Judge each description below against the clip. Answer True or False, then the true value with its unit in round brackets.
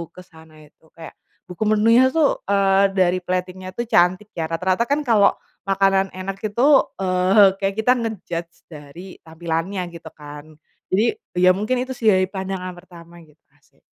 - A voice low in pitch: False (185 Hz)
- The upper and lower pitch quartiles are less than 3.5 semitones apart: True (2.8 semitones)